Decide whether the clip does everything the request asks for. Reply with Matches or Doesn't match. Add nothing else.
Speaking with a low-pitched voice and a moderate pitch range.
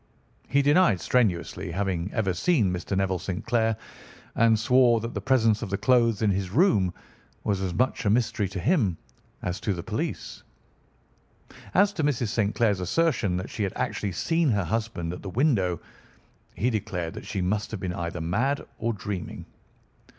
Matches